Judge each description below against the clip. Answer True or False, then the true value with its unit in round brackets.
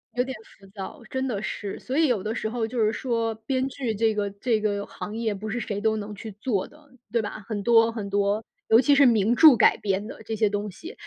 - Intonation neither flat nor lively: True (3.0 semitones)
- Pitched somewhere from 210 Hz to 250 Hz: True (220 Hz)